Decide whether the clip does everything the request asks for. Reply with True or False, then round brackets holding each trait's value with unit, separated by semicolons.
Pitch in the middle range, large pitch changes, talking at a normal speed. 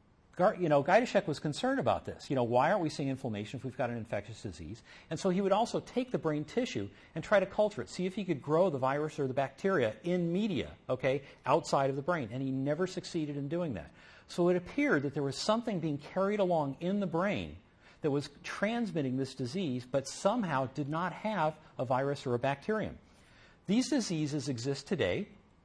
False (150 Hz; 5.7 semitones; 210 wpm)